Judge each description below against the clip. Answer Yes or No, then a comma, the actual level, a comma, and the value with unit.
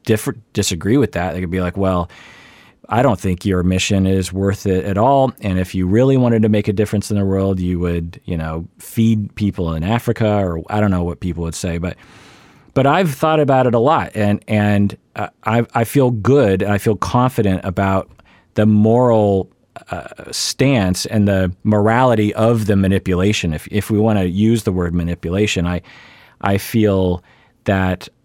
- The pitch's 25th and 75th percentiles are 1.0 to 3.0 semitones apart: No, average, 3.4 semitones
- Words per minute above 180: Yes, average, 190 wpm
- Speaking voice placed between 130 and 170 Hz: No, low, 100 Hz